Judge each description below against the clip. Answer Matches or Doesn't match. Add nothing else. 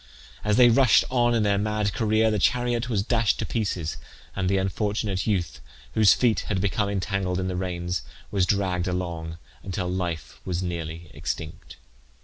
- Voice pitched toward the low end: Matches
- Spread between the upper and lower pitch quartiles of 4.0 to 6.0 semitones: Doesn't match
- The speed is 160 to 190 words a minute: Matches